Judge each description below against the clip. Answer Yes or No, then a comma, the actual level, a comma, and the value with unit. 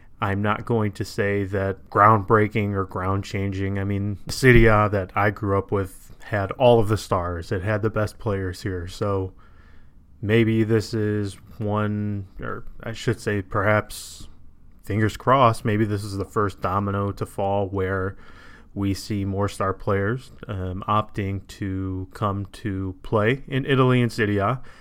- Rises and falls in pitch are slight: Yes, narrow, 2.1 semitones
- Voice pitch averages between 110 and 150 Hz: No, low, 100 Hz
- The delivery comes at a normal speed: Yes, average, 155 wpm